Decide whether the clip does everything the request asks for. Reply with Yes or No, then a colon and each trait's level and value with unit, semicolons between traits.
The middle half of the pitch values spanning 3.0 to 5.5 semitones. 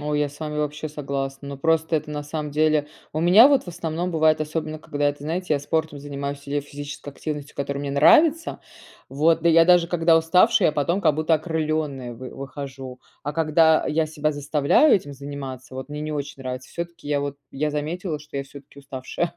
No: narrow, 2.4 semitones